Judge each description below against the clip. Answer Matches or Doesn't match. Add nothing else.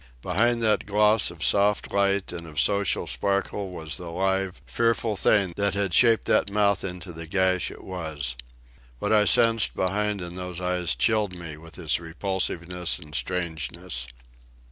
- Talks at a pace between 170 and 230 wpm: Doesn't match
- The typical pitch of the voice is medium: Doesn't match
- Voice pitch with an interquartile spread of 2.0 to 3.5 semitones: Matches